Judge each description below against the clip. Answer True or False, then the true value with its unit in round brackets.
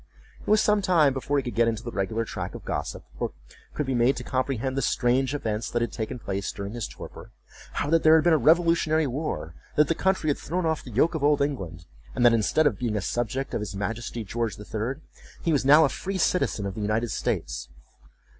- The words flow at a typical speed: False (230 wpm)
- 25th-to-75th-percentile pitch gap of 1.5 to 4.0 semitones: False (5.6 semitones)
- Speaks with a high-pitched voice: False (130 Hz)